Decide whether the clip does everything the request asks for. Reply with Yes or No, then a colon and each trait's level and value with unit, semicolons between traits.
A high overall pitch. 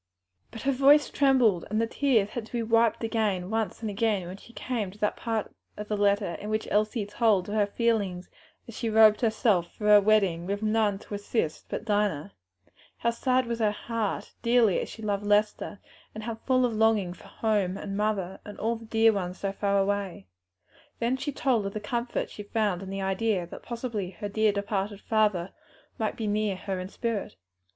Yes: high, 210 Hz